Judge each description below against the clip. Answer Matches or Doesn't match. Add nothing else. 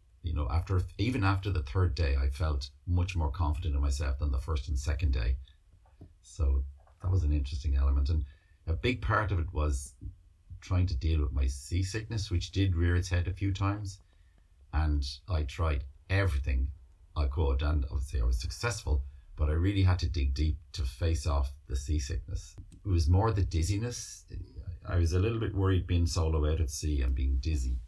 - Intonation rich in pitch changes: Doesn't match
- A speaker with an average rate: Matches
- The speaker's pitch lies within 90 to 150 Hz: Doesn't match